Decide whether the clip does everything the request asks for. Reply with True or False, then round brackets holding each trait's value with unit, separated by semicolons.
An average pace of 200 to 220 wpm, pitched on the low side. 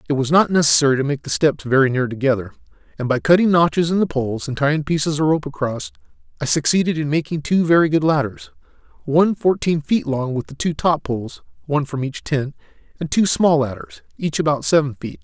False (205 wpm; 150 Hz)